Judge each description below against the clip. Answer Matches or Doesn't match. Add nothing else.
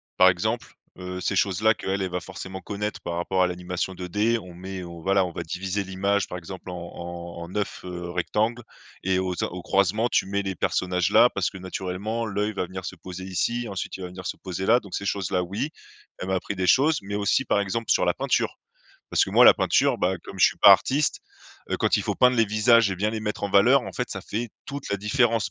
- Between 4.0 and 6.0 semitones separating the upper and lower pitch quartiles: Doesn't match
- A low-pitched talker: Matches